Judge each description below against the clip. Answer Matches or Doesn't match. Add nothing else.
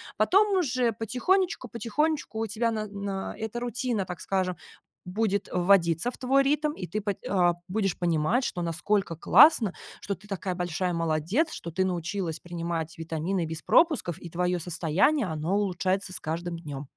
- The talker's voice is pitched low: Doesn't match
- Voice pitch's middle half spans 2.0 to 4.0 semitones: Doesn't match